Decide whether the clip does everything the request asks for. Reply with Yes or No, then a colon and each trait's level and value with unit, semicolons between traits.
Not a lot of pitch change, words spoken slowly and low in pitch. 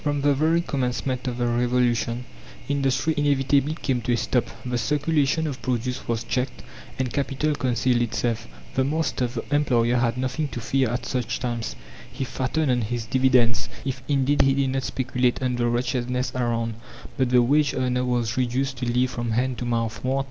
No: narrow, 2.0 semitones; average, 180 wpm; low, 125 Hz